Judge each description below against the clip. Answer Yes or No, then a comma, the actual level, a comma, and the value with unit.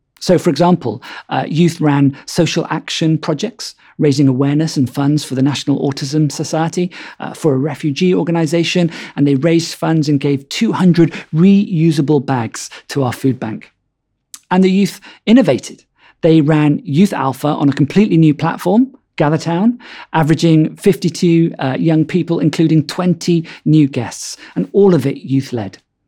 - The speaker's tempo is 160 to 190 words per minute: No, average, 150 wpm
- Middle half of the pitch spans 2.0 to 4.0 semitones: Yes, average, 3.4 semitones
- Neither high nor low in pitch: Yes, medium, 160 Hz